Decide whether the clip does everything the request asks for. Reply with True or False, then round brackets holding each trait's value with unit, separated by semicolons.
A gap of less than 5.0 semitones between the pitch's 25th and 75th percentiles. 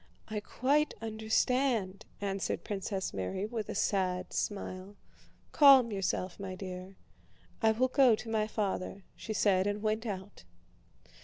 True (2.8 semitones)